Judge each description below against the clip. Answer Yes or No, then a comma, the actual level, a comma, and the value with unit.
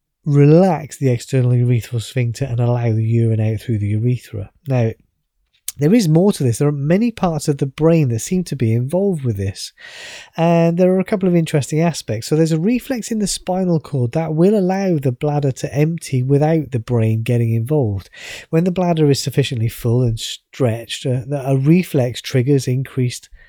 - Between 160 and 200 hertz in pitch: No, medium, 140 Hz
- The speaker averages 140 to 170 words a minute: No, average, 185 wpm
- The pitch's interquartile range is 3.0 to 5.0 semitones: No, wide, 5.4 semitones